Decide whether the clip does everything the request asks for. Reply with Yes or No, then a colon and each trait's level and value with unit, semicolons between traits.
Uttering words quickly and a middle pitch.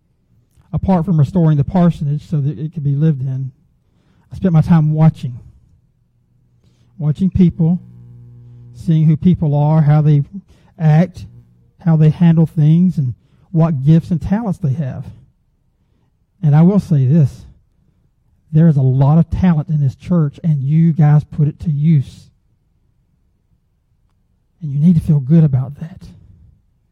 No: average, 145 wpm; medium, 155 Hz